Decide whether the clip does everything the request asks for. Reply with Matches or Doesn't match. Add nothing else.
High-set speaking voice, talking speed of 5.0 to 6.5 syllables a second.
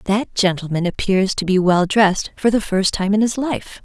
Doesn't match